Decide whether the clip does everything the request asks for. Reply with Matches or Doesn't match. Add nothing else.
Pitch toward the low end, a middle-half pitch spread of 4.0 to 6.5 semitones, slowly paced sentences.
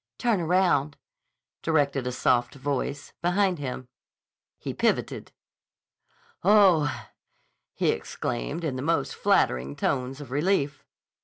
Doesn't match